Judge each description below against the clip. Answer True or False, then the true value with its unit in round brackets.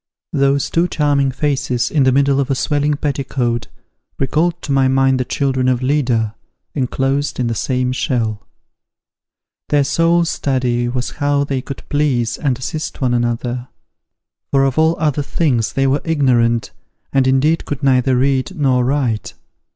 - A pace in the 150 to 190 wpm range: True (155 wpm)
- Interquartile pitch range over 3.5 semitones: False (2.4 semitones)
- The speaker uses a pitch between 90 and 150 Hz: True (135 Hz)